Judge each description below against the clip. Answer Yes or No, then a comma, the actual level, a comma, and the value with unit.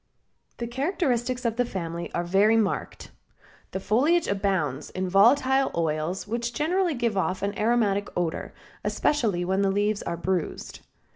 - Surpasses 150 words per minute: No, average, 145 wpm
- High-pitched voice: Yes, high, 205 Hz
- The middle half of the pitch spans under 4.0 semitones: No, average, 4.5 semitones